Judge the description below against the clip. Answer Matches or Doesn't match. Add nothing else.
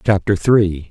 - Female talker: Doesn't match